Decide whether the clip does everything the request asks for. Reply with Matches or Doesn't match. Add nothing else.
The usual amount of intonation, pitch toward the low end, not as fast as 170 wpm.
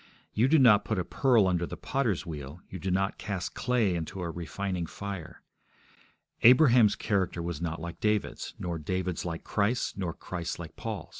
Doesn't match